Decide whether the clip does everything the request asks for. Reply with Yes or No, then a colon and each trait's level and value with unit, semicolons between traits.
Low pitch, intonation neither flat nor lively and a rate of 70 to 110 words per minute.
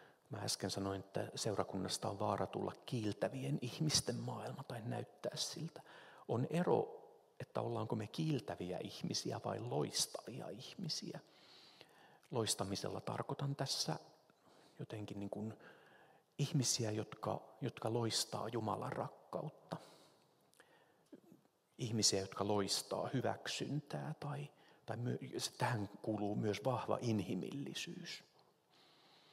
No: low, 120 Hz; wide, 5.7 semitones; average, 100 wpm